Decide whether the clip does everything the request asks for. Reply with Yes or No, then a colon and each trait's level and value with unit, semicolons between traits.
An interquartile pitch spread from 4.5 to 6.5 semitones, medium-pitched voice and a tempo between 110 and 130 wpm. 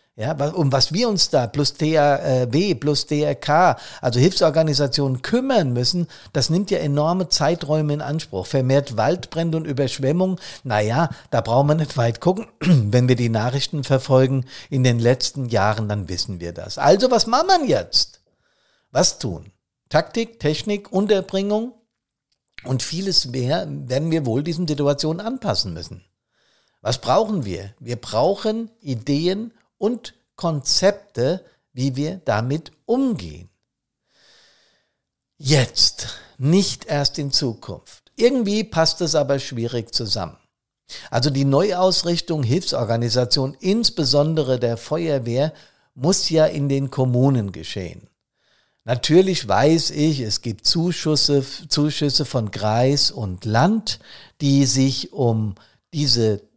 Yes: average, 5.2 semitones; medium, 145 Hz; slow, 125 wpm